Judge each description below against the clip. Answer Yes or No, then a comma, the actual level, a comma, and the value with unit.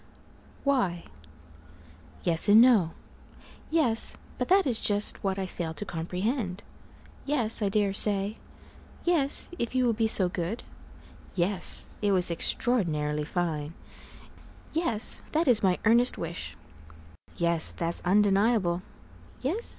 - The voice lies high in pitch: Yes, high, 205 Hz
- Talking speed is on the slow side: Yes, slow, 120 wpm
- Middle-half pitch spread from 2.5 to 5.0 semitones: No, wide, 5.4 semitones